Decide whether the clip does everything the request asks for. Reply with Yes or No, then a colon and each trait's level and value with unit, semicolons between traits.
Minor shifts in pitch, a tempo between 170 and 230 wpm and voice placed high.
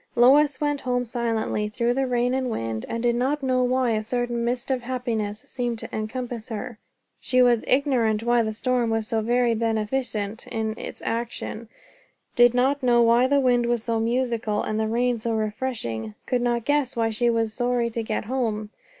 Yes: narrow, 2.1 semitones; average, 190 wpm; high, 235 Hz